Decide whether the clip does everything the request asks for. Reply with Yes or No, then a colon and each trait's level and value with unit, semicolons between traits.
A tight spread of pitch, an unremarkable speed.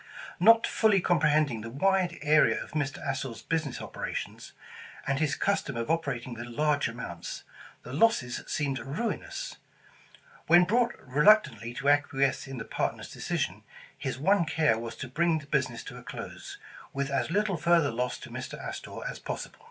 No: average, 5.1 semitones; average, 165 wpm